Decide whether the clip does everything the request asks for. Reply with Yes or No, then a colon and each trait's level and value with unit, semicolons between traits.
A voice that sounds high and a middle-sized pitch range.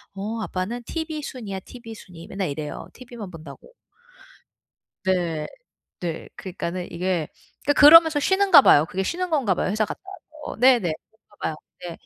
No: high, 205 Hz; wide, 7.2 semitones